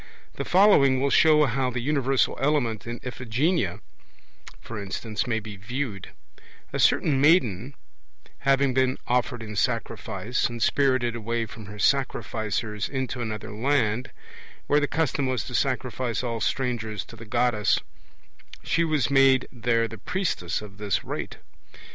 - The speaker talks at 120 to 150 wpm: Yes, average, 140 wpm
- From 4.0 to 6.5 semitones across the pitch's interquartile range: No, average, 3.6 semitones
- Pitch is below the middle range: Yes, low, 125 Hz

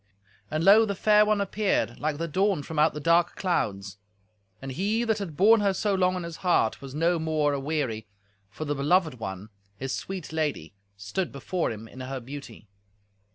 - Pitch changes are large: Yes, wide, 5.9 semitones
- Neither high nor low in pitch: Yes, medium, 160 Hz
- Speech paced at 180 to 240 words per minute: Yes, average, 190 wpm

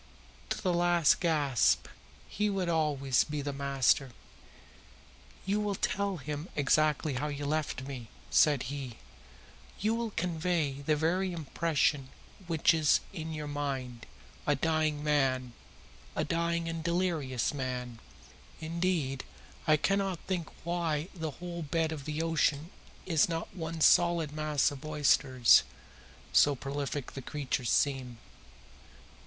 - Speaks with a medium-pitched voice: Yes, medium, 155 Hz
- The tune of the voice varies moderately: Yes, average, 3.4 semitones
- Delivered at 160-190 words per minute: No, slow, 135 wpm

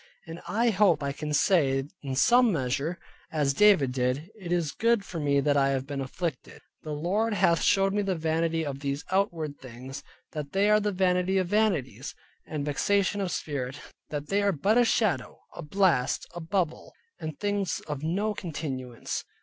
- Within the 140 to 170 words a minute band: No, average, 180 wpm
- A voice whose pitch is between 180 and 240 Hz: No, medium, 165 Hz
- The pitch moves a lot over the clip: Yes, wide, 5.7 semitones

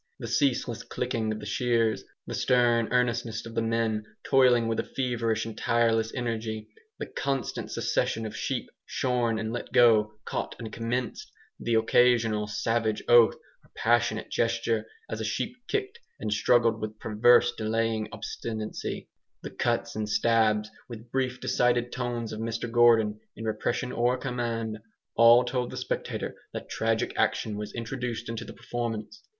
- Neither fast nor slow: Yes, average, 155 wpm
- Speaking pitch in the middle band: No, low, 115 Hz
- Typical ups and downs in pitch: No, narrow, 1.7 semitones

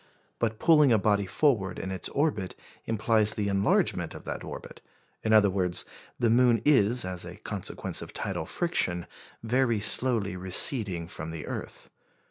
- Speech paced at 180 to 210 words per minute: No, average, 155 wpm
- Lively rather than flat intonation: No, average, 4.3 semitones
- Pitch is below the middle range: Yes, low, 105 Hz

